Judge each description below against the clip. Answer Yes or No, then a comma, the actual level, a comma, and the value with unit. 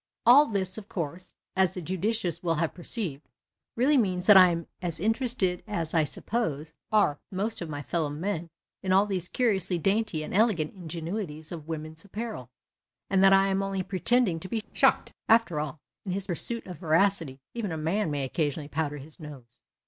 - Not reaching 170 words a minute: No, average, 185 wpm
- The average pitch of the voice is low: No, medium, 180 Hz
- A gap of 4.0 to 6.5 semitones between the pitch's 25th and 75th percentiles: Yes, average, 4.3 semitones